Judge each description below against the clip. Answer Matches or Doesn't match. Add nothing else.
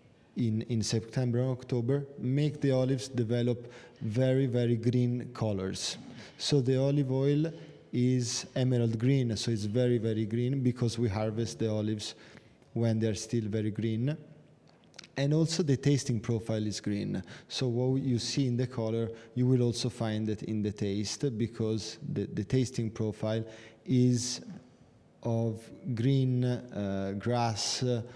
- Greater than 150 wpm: Doesn't match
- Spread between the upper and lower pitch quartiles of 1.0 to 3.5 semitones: Matches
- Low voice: Matches